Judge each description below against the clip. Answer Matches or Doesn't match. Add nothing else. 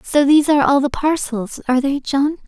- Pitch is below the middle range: Doesn't match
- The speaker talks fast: Matches